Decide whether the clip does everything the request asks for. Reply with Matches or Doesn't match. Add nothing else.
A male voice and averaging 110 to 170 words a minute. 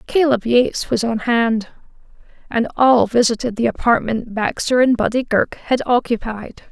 Doesn't match